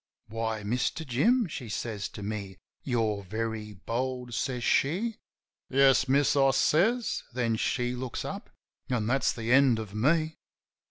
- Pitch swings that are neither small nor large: Yes, average, 3.7 semitones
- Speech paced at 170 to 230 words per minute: No, average, 150 wpm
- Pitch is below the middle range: Yes, low, 125 Hz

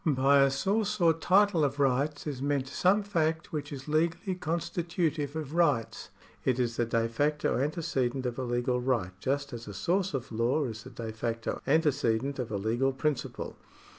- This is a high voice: No, medium, 140 Hz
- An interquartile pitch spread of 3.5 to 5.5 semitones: Yes, average, 4.7 semitones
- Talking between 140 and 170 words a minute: No, average, 180 wpm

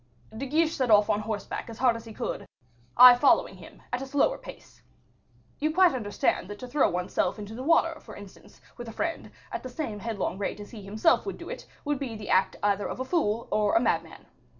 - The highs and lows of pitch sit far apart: No, average, 4.9 semitones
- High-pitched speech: Yes, high, 230 Hz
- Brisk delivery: Yes, fast, 230 wpm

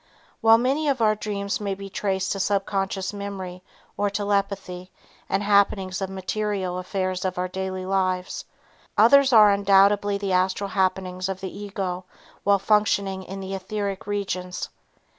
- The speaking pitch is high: Yes, high, 195 Hz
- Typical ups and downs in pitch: No, narrow, 1.5 semitones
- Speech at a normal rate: Yes, average, 145 wpm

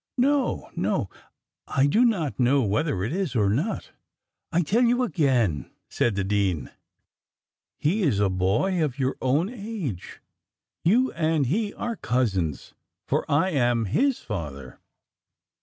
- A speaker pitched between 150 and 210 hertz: No, medium, 140 Hz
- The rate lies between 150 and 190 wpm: No, average, 140 wpm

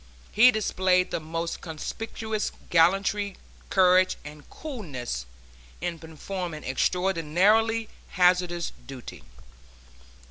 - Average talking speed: No, slow, 80 wpm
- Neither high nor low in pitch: Yes, medium, 180 Hz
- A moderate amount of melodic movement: Yes, average, 3.8 semitones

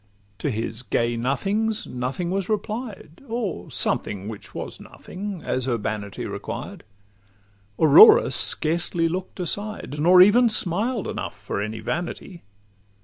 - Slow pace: Yes, slow, 120 wpm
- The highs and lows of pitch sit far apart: Yes, wide, 9.0 semitones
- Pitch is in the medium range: Yes, medium, 175 Hz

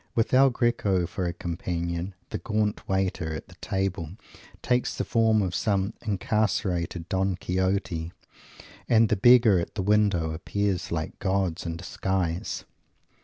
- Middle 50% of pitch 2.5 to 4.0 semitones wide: Yes, average, 3.5 semitones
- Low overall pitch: Yes, very low, 95 Hz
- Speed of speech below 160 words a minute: Yes, average, 140 wpm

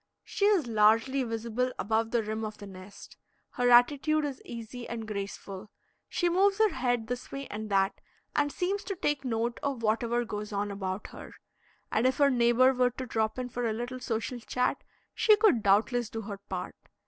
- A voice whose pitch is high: Yes, high, 240 Hz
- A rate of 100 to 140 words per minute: No, average, 190 wpm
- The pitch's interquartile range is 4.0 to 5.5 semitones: No, average, 3.3 semitones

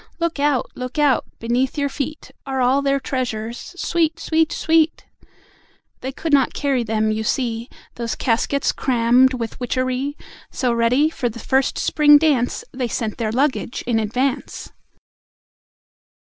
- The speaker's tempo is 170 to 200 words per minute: No, average, 145 wpm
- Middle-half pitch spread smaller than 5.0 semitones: Yes, average, 3.4 semitones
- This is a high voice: Yes, very high, 260 Hz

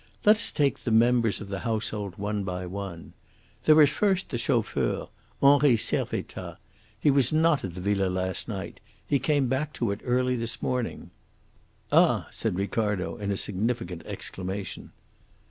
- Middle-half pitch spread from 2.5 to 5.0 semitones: No, wide, 5.4 semitones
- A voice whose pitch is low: Yes, low, 115 Hz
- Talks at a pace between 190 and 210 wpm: No, average, 160 wpm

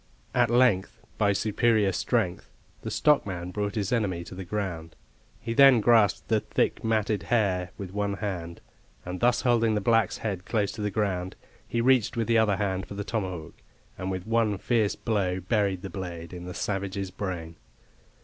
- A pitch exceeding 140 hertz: No, low, 100 Hz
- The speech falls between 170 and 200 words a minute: Yes, average, 180 wpm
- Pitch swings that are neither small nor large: Yes, average, 3.4 semitones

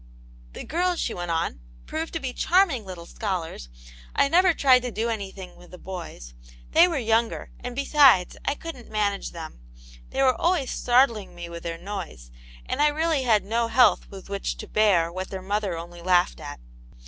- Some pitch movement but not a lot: No, wide, 7.3 semitones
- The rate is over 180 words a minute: Yes, average, 195 wpm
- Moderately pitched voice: No, high, 210 Hz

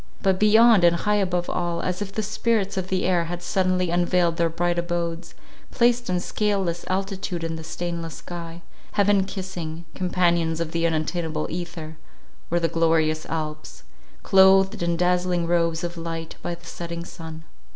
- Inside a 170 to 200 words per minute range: No, average, 160 wpm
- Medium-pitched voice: Yes, medium, 175 Hz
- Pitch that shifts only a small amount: Yes, narrow, 2.1 semitones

